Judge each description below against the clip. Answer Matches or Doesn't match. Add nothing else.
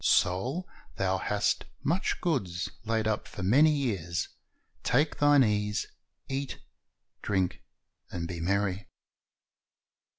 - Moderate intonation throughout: Doesn't match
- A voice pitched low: Matches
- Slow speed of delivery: Matches